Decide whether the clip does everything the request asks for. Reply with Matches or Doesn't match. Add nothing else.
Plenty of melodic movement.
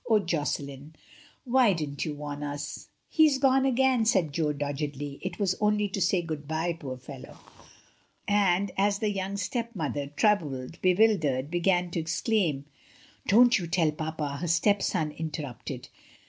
Matches